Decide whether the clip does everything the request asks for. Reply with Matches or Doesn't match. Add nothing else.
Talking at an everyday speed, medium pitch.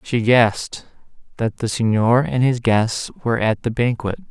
Doesn't match